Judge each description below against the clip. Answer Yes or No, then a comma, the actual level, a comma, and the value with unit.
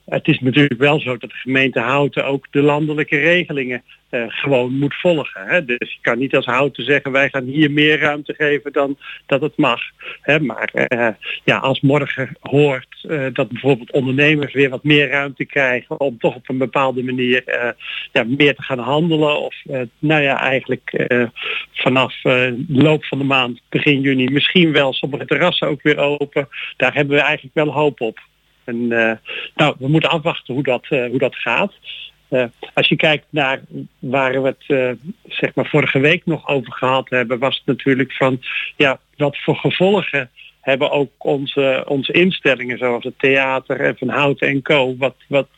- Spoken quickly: No, average, 190 wpm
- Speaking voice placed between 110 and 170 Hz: Yes, medium, 140 Hz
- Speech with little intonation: Yes, narrow, 2.2 semitones